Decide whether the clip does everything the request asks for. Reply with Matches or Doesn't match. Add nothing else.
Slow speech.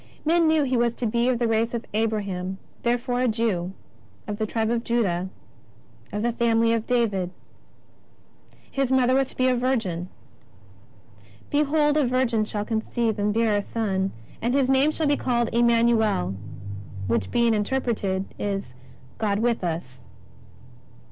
Doesn't match